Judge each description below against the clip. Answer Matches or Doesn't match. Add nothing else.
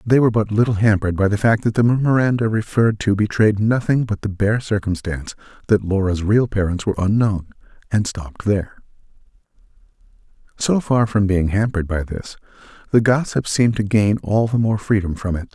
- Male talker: Matches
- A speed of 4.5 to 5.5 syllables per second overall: Doesn't match